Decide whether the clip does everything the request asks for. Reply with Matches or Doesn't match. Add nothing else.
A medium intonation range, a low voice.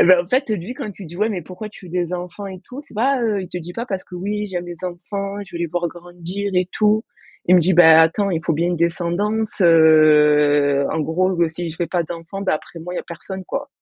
Doesn't match